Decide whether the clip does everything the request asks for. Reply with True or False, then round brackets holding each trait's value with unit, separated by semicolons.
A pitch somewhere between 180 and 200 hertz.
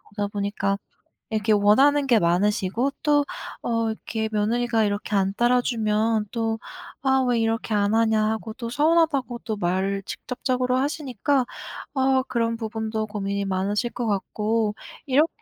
False (225 Hz)